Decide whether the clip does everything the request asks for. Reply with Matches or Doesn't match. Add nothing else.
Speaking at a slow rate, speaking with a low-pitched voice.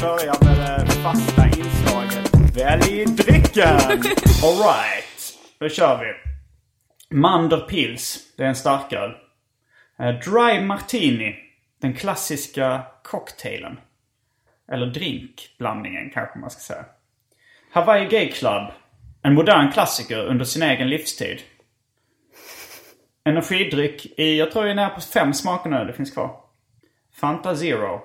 Doesn't match